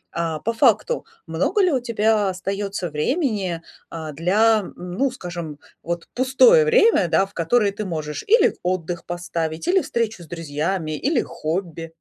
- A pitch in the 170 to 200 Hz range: Yes, medium, 185 Hz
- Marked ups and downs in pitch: Yes, wide, 6.0 semitones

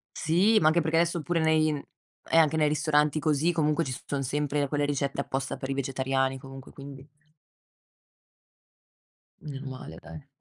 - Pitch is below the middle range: No, medium, 145 Hz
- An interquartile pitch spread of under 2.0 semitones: No, average, 2.8 semitones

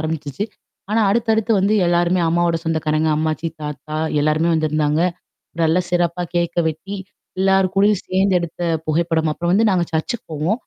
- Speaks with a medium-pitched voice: Yes, medium, 170 Hz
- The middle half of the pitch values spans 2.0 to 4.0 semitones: Yes, average, 3.3 semitones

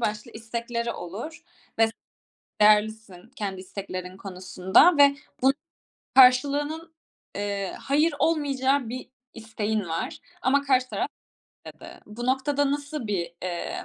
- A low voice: No, high, 235 Hz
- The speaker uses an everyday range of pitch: No, wide, 5.7 semitones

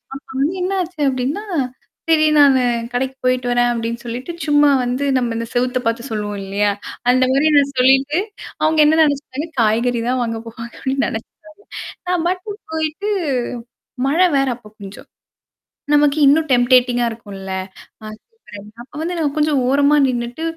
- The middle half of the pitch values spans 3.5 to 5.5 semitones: Yes, average, 4.3 semitones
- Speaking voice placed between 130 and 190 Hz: No, very high, 265 Hz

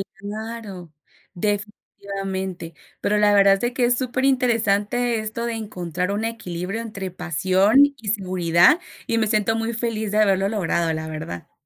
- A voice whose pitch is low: No, high, 205 Hz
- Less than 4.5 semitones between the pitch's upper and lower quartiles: Yes, average, 3.5 semitones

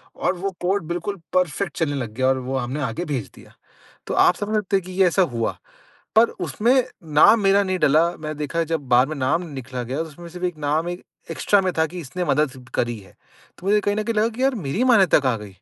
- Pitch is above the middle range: No, medium, 165 Hz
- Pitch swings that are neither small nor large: No, wide, 6.3 semitones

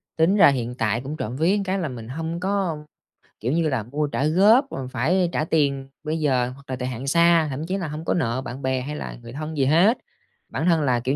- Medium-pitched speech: Yes, medium, 150 Hz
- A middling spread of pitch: Yes, average, 4.4 semitones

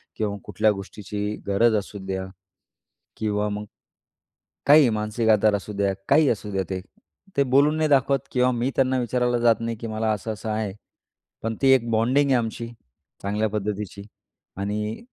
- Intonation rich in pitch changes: No, average, 3.1 semitones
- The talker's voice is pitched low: Yes, low, 110 Hz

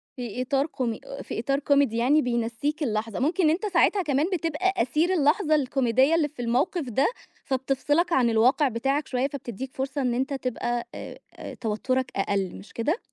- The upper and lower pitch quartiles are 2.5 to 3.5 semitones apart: No, average, 4.0 semitones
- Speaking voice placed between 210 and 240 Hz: No, very high, 270 Hz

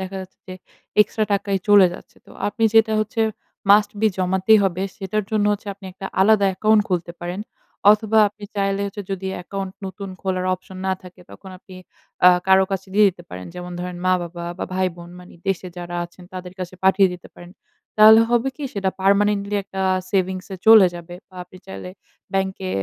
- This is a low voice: No, high, 190 Hz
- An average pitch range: No, narrow, 2.1 semitones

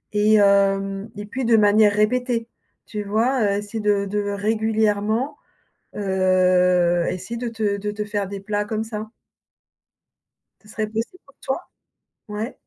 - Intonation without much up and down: Yes, narrow, 1.8 semitones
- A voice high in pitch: Yes, high, 210 Hz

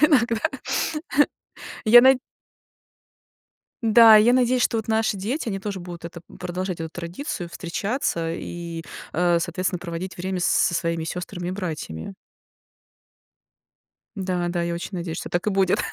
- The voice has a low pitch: No, medium, 185 Hz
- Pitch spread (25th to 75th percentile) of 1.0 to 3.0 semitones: No, average, 4.0 semitones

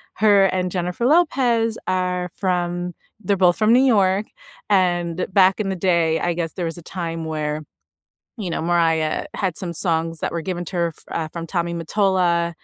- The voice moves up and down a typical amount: No, narrow, 2.3 semitones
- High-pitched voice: No, medium, 180 Hz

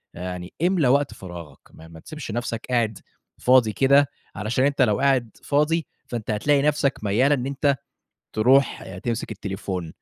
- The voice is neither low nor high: No, low, 125 Hz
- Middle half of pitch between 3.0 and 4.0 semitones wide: No, average, 5.1 semitones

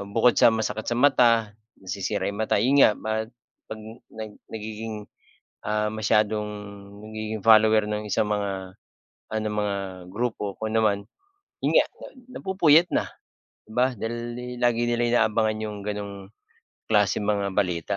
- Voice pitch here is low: Yes, low, 110 Hz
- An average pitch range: No, narrow, 1.6 semitones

